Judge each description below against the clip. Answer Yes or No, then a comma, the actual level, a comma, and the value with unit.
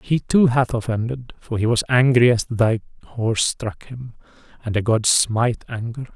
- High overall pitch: No, low, 120 Hz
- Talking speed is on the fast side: No, average, 175 wpm